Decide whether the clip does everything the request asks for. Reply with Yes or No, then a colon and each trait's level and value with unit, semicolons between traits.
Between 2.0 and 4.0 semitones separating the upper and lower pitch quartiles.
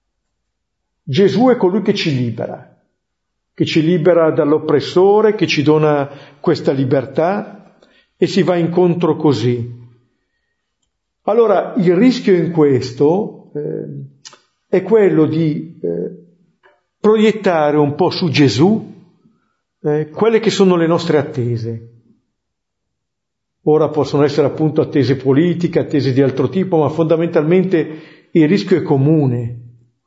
No: average, 4.5 semitones